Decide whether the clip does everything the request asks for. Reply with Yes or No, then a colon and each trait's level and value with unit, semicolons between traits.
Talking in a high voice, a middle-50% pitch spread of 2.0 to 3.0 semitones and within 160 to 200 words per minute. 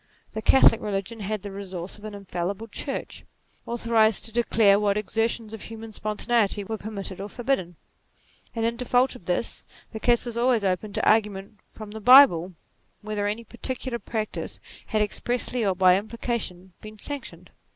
Yes: high, 215 Hz; average, 2.7 semitones; average, 165 wpm